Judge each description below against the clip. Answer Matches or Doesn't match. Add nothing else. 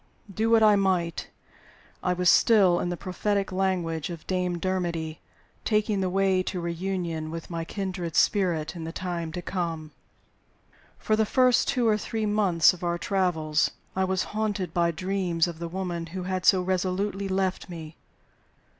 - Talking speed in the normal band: Matches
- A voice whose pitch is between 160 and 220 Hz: Matches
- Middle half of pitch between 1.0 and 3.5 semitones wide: Matches